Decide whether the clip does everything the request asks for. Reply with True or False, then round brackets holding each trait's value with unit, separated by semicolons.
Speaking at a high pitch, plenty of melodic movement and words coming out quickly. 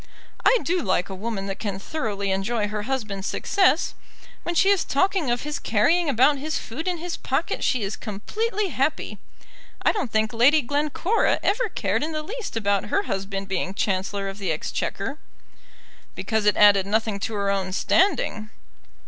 False (225 Hz; 7.9 semitones; 175 wpm)